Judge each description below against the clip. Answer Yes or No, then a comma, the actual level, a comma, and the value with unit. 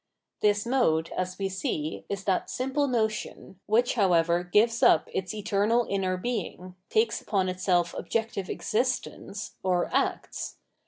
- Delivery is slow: Yes, slow, 130 wpm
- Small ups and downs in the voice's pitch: No, average, 4.0 semitones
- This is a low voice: No, high, 200 Hz